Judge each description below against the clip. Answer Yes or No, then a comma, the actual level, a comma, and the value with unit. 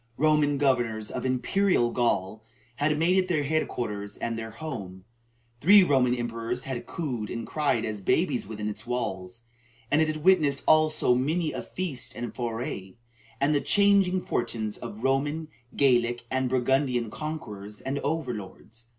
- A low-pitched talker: Yes, low, 130 Hz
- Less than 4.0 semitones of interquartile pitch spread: No, average, 5.1 semitones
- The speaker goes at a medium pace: Yes, average, 155 wpm